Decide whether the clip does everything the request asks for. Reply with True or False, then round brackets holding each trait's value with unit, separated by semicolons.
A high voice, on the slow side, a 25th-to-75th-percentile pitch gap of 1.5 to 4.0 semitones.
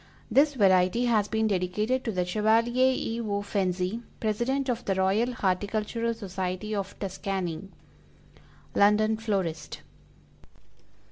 True (210 Hz; 115 wpm; 3.4 semitones)